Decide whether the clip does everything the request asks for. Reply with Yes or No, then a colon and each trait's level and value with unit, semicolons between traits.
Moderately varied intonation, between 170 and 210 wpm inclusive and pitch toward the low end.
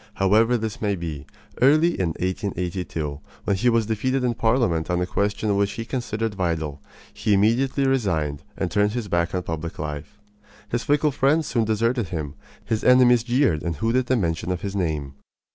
No: wide, 5.9 semitones; average, 180 wpm; low, 105 Hz